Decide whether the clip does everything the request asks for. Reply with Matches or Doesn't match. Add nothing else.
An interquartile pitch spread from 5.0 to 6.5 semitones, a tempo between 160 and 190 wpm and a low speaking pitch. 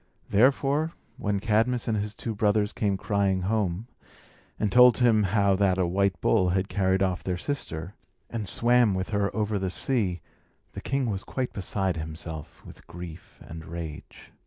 Doesn't match